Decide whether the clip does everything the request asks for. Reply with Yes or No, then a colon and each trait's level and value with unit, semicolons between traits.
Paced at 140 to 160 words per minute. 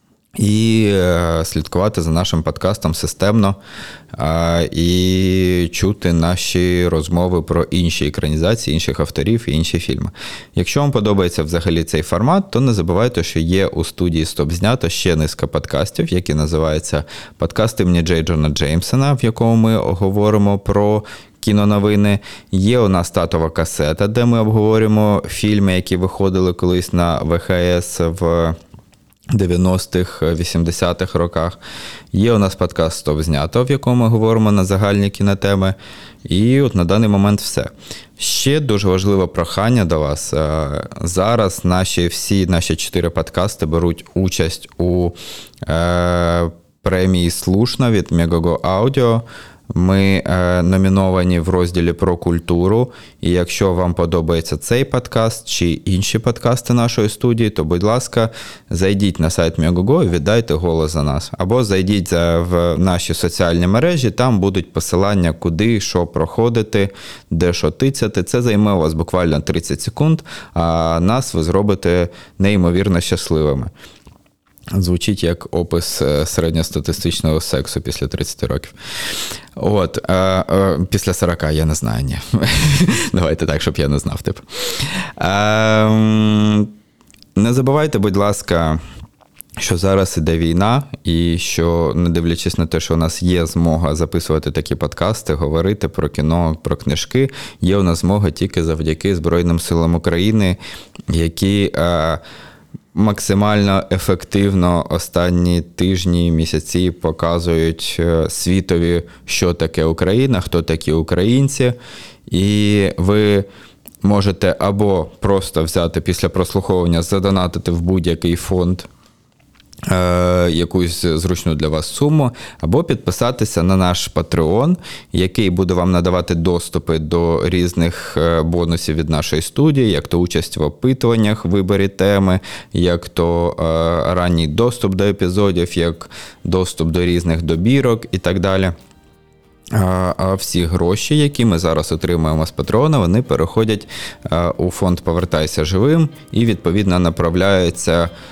No: average, 125 wpm